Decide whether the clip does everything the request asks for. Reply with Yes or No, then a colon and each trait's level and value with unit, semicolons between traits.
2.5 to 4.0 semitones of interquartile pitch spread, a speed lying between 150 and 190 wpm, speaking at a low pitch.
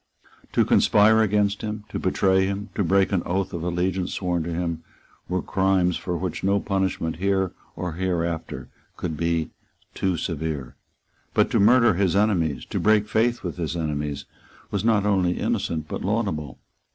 Yes: average, 3.1 semitones; average, 165 wpm; very low, 95 Hz